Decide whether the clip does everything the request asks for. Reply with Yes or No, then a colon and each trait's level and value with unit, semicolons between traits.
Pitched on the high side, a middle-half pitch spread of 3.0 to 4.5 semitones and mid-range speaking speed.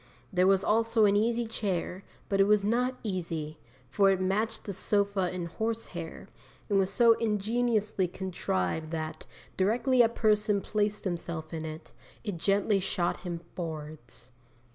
Yes: high, 195 Hz; average, 4.1 semitones; average, 150 wpm